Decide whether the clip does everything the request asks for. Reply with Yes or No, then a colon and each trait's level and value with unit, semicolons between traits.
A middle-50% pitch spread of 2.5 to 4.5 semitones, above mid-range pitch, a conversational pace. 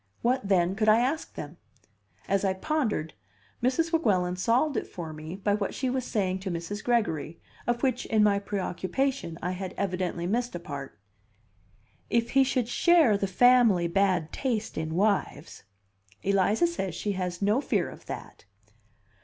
No: average, 5.2 semitones; high, 200 Hz; average, 165 wpm